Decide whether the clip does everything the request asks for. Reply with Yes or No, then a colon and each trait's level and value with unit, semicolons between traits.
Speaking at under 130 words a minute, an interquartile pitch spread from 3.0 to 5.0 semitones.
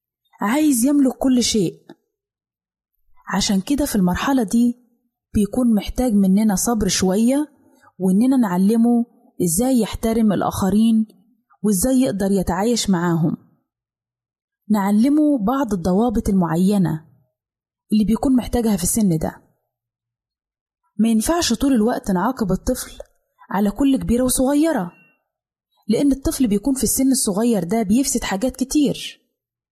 Yes: average, 105 wpm; average, 4.7 semitones